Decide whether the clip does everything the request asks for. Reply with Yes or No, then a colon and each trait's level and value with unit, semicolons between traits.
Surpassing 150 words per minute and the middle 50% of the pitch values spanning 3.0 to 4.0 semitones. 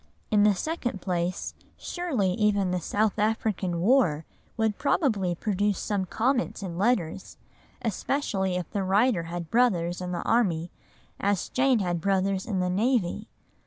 No: average, 145 wpm; average, 3.7 semitones